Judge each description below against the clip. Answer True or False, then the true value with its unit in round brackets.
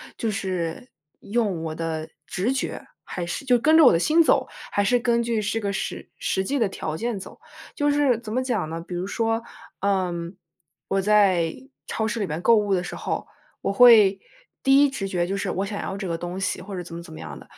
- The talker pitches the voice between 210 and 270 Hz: False (200 Hz)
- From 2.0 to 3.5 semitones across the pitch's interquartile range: False (4.9 semitones)